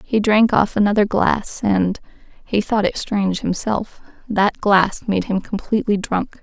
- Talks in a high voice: Yes, high, 205 Hz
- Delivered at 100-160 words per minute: Yes, average, 140 wpm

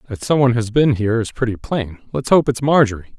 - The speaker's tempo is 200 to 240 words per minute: Yes, fast, 205 wpm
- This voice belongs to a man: Yes, male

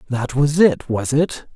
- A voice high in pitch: No, low, 135 Hz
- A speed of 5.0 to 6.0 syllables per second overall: No, 3.8 syllables/s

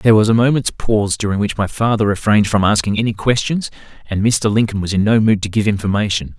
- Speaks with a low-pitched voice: Yes, low, 105 Hz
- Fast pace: Yes, fast, 225 wpm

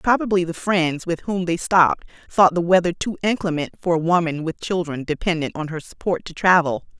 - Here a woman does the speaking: Yes, female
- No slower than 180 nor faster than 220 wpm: Yes, average, 195 wpm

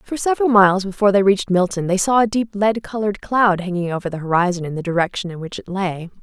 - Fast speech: Yes, fast, 240 wpm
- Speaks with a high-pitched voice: Yes, high, 195 Hz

